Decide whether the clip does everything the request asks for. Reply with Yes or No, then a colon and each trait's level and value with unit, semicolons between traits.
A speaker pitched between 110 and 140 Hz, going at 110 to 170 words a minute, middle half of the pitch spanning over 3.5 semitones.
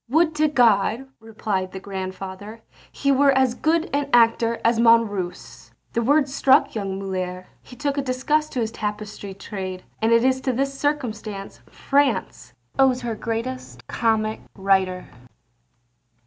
No: high, 230 Hz; average, 145 wpm; average, 5.1 semitones